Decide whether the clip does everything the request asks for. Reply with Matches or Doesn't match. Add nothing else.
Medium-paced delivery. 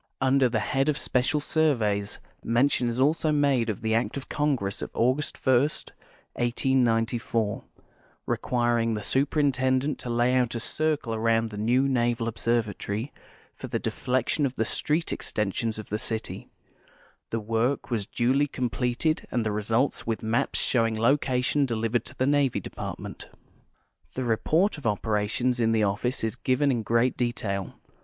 Matches